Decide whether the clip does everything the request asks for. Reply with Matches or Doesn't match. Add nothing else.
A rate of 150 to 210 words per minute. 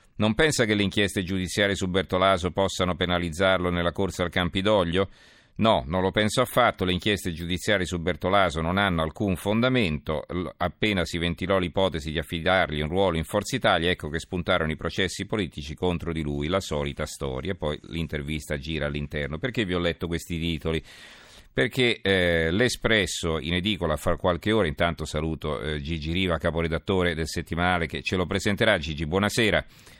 Matches